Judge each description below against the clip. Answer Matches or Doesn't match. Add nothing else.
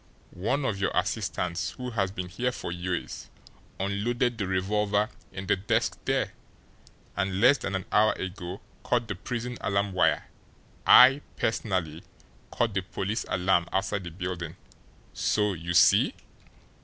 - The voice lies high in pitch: Doesn't match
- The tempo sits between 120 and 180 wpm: Matches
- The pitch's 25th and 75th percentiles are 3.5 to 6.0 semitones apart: Doesn't match